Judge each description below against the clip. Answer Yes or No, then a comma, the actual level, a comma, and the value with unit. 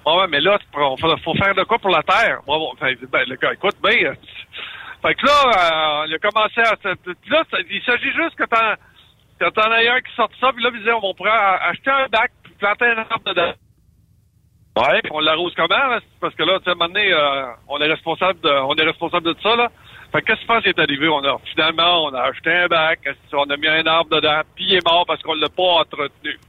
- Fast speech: Yes, fast, 240 wpm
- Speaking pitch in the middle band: Yes, medium, 170 Hz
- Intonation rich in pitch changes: Yes, wide, 5.7 semitones